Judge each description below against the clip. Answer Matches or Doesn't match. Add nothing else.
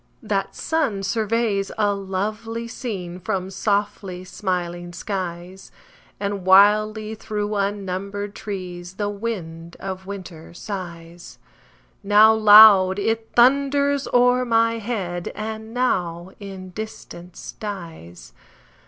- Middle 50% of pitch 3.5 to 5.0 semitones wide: Doesn't match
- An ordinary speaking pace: Doesn't match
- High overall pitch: Matches